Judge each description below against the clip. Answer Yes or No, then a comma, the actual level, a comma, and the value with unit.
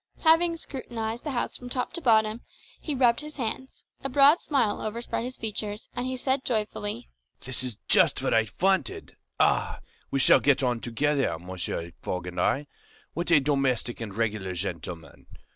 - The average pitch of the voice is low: No, high, 210 Hz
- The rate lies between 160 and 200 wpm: Yes, average, 170 wpm